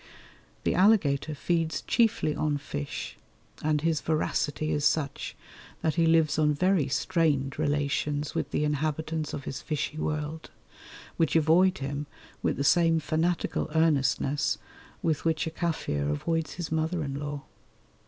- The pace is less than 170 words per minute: Yes, average, 140 wpm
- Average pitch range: No, narrow, 2.0 semitones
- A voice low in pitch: No, medium, 155 Hz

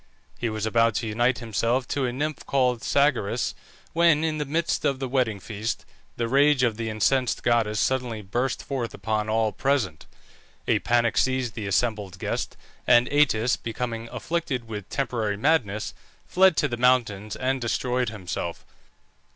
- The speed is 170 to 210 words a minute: No, average, 160 wpm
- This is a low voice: Yes, low, 120 Hz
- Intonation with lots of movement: No, average, 3.4 semitones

